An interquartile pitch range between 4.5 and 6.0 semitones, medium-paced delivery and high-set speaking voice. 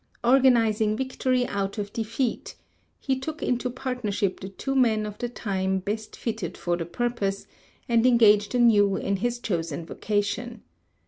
No: average, 3.5 semitones; average, 145 wpm; high, 220 Hz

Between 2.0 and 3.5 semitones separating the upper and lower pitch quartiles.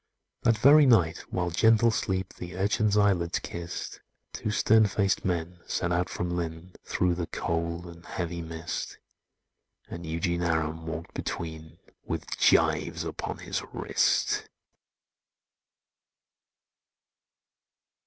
Yes: average, 2.7 semitones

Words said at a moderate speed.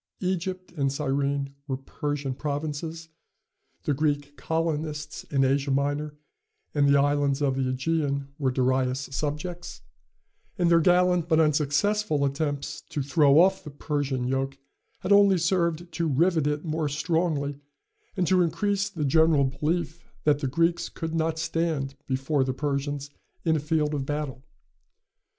Yes: average, 145 wpm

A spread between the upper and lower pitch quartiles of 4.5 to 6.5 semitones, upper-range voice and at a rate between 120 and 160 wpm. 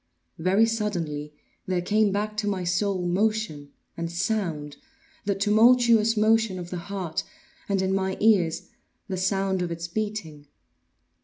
No: average, 3.7 semitones; high, 195 Hz; slow, 135 wpm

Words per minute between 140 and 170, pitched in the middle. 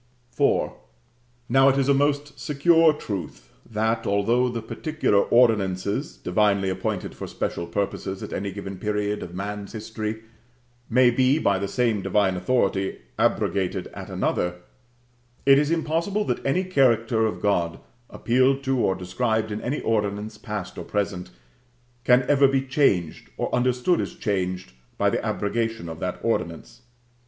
No: average, 145 wpm; low, 110 Hz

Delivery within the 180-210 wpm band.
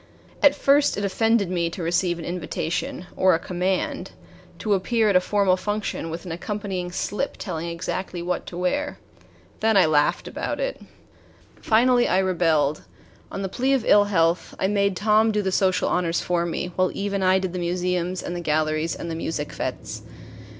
Yes: average, 185 wpm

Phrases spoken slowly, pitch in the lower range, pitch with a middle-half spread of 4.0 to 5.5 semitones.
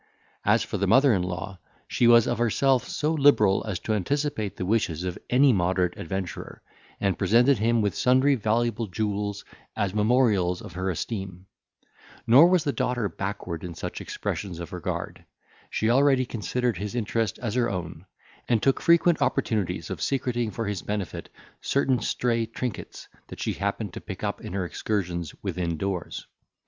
No: average, 165 wpm; low, 110 Hz; average, 4.9 semitones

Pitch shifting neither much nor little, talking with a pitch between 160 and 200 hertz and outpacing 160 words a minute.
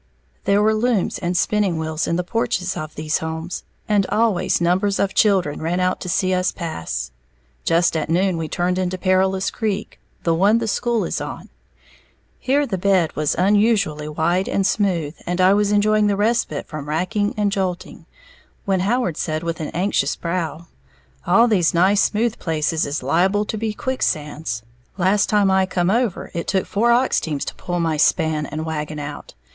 Yes: average, 4.2 semitones; medium, 185 Hz; average, 180 wpm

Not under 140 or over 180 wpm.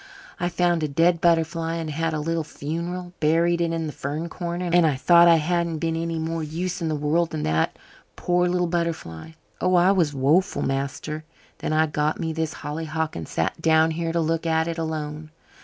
No: fast, 205 wpm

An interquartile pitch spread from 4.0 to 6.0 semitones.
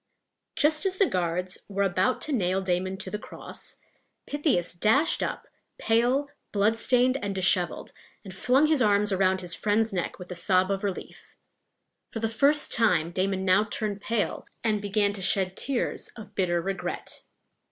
No: average, 3.5 semitones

